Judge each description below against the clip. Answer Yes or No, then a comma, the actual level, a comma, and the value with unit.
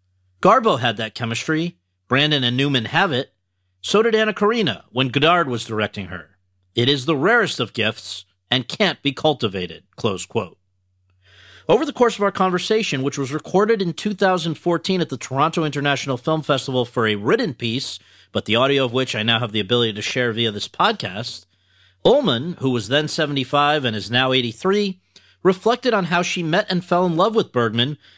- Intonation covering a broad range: Yes, wide, 8.0 semitones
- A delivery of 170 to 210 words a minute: Yes, average, 185 wpm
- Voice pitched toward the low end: Yes, low, 130 Hz